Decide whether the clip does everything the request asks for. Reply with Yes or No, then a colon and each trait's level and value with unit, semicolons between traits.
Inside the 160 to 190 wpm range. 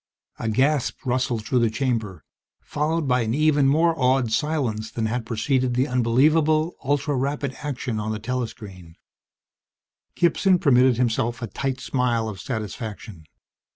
No: average, 145 wpm